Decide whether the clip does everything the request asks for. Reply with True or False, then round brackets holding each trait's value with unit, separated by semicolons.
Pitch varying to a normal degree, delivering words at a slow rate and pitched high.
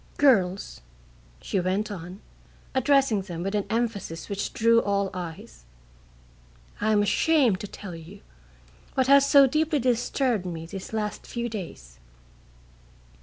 True (4.8 semitones; 130 wpm; 205 Hz)